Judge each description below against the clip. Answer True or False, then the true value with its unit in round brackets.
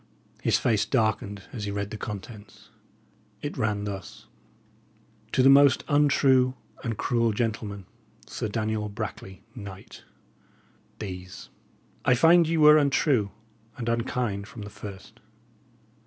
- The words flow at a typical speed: False (125 wpm)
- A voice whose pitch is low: True (110 Hz)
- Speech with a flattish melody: False (4.1 semitones)